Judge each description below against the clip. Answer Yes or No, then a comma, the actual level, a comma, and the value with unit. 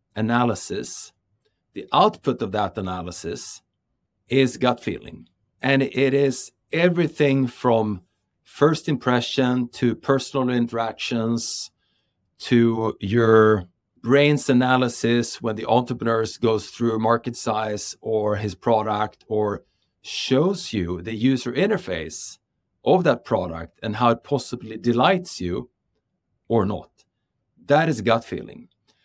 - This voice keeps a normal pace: No, slow, 115 wpm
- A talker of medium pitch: No, low, 115 Hz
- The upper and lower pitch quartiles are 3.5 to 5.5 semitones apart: No, average, 3.0 semitones